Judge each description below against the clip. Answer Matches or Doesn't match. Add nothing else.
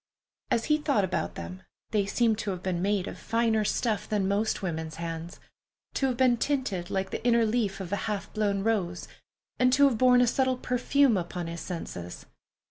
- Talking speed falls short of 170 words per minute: Doesn't match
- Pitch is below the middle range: Doesn't match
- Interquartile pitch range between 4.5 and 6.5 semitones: Matches